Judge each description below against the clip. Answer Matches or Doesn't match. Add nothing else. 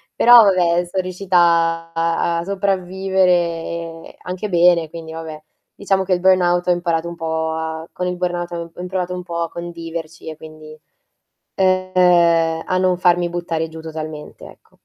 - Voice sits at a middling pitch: Matches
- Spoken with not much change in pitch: Matches